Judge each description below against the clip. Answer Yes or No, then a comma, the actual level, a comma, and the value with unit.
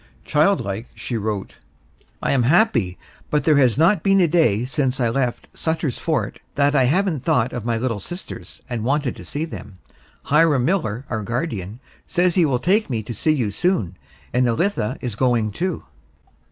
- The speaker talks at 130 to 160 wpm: No, average, 180 wpm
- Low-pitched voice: Yes, low, 130 Hz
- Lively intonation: Yes, wide, 6.0 semitones